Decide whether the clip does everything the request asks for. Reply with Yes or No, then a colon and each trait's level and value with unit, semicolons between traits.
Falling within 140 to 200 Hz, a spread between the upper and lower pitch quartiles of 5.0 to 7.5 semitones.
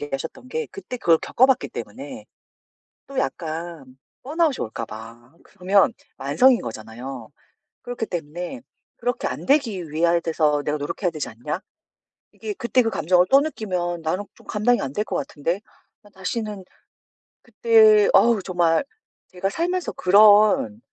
No: medium, 185 Hz; wide, 8.0 semitones